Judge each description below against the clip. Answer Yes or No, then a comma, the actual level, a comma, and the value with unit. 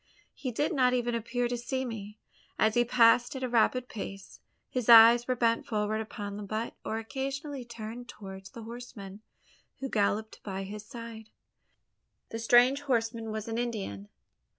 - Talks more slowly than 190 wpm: Yes, average, 165 wpm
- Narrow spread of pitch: Yes, narrow, 2.3 semitones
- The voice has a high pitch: Yes, high, 230 Hz